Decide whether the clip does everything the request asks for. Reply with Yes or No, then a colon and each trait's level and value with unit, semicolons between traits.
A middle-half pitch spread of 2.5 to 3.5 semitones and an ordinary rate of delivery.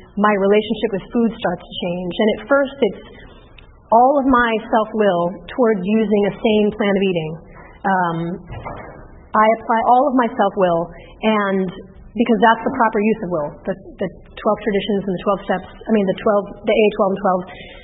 Yes: average, 3.1 semitones; average, 190 wpm